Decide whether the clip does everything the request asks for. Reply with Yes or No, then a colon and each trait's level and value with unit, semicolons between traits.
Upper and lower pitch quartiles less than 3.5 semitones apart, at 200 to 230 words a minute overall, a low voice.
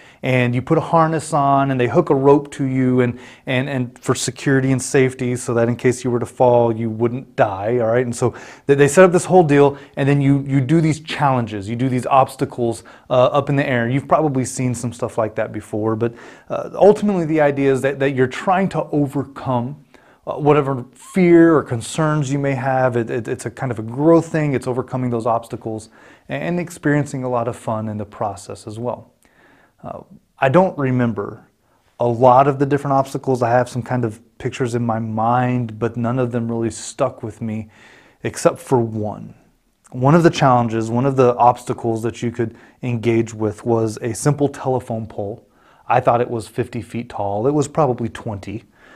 Yes: average, 3.1 semitones; fast, 205 wpm; low, 125 Hz